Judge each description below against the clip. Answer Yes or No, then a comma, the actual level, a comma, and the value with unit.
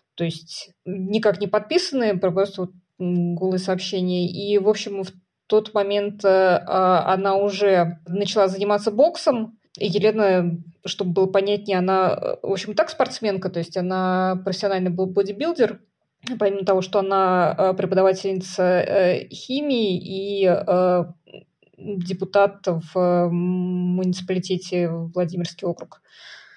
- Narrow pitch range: Yes, narrow, 1.9 semitones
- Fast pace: No, average, 120 wpm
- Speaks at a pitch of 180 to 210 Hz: Yes, high, 190 Hz